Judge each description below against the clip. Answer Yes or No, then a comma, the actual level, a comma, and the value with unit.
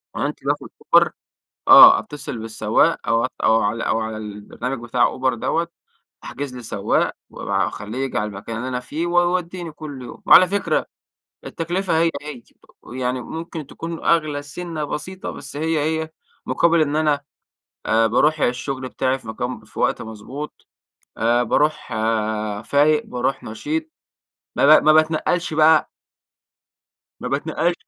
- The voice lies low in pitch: No, medium, 145 Hz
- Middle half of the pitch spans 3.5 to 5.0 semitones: No, wide, 5.6 semitones